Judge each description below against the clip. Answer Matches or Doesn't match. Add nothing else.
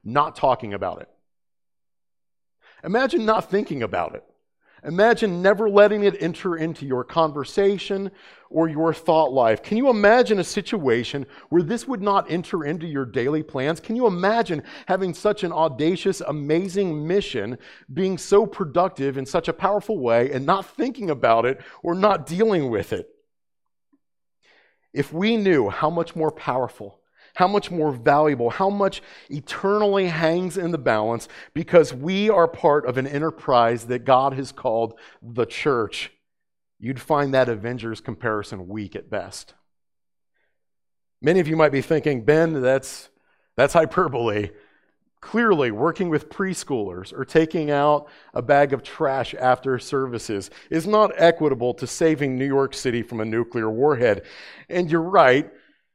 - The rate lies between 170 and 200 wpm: Doesn't match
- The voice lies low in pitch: Doesn't match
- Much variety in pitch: Matches